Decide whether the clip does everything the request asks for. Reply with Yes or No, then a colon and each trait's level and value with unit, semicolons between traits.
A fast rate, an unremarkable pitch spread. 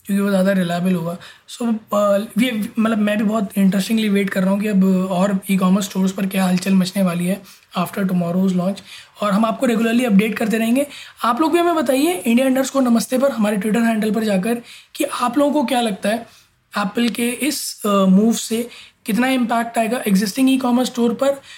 Yes: fast, 205 wpm; average, 3.6 semitones